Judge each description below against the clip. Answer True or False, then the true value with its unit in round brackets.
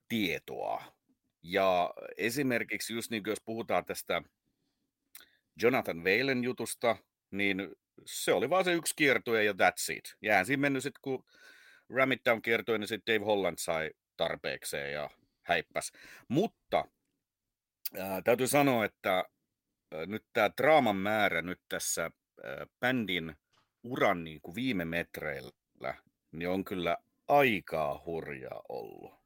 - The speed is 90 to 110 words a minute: False (130 wpm)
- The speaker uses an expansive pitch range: True (5.9 semitones)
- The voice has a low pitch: True (115 Hz)